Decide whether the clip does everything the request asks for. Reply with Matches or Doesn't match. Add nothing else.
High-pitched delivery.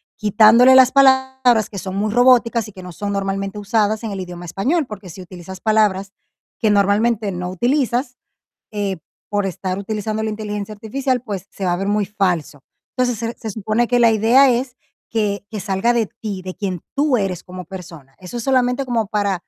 Matches